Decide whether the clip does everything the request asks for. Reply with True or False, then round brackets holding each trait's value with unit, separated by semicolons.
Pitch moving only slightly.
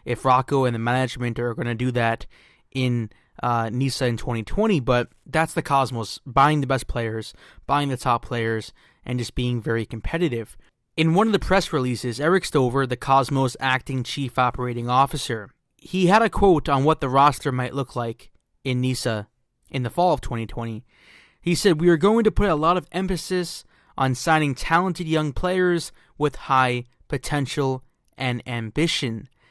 False (4.7 semitones)